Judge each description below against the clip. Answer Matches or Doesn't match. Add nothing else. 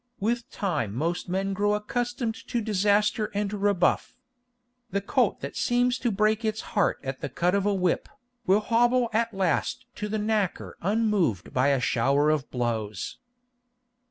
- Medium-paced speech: Matches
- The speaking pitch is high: Matches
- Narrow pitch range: Doesn't match